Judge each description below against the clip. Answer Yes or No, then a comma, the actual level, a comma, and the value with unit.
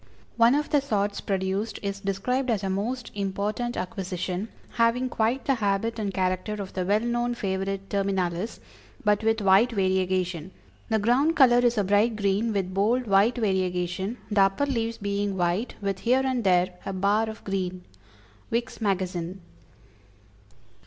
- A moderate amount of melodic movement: Yes, average, 3.4 semitones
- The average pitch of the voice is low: No, high, 200 Hz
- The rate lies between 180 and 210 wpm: No, average, 155 wpm